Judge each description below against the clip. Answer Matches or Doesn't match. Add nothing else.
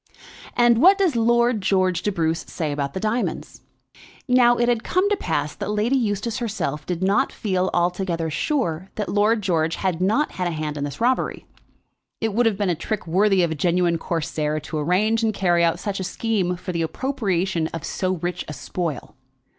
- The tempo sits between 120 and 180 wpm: Doesn't match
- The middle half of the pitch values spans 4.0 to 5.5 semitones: Matches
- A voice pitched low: Doesn't match